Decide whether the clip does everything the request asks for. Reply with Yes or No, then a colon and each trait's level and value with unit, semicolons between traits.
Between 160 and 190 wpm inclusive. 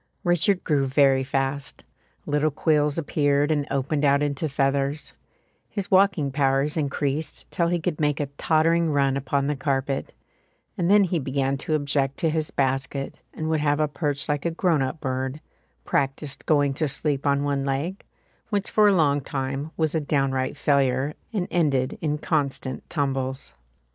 Yes: average, 165 wpm